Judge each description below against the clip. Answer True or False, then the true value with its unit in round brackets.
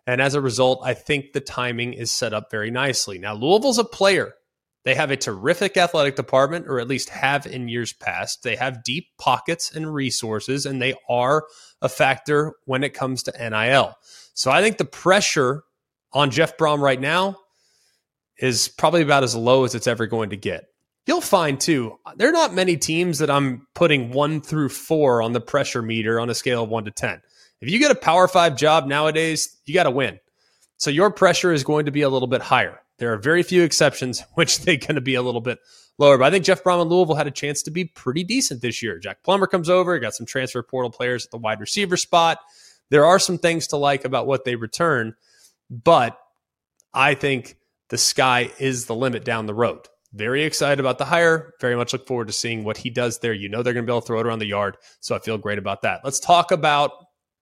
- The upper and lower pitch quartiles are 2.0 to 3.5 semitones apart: False (4.8 semitones)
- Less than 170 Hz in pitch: True (135 Hz)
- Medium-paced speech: False (225 wpm)